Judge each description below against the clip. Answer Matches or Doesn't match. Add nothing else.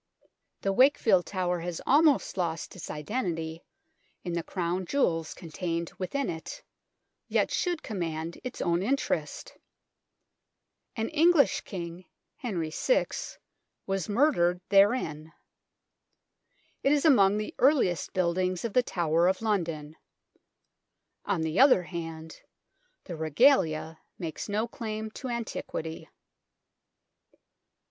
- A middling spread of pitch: Doesn't match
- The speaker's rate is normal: Doesn't match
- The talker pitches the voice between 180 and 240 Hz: Matches